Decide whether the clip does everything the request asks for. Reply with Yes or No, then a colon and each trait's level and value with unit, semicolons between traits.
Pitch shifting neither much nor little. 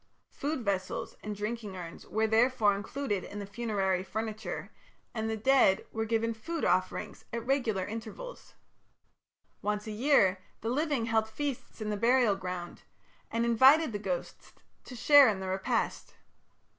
Yes: average, 3.3 semitones